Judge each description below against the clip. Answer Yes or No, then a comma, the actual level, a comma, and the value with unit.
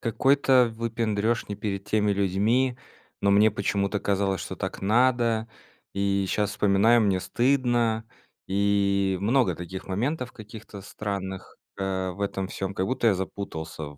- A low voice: Yes, low, 100 Hz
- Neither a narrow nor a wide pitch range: Yes, average, 3.0 semitones